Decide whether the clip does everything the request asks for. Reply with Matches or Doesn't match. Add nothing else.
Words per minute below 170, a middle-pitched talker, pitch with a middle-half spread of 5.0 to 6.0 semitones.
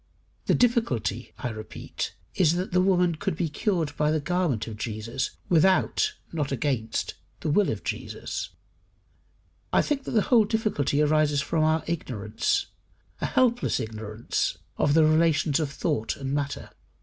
Matches